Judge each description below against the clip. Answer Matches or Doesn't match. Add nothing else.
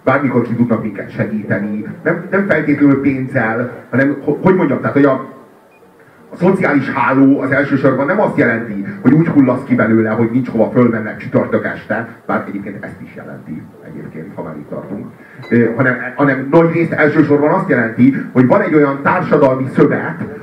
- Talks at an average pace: Doesn't match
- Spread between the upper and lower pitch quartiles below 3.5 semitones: Doesn't match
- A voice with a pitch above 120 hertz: Matches